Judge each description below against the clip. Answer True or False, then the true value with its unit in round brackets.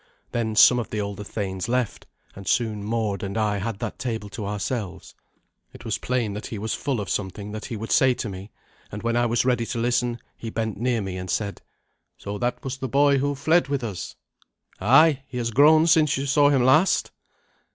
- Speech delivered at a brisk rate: True (215 wpm)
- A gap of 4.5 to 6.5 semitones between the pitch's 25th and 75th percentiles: False (4.0 semitones)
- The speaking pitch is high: False (115 Hz)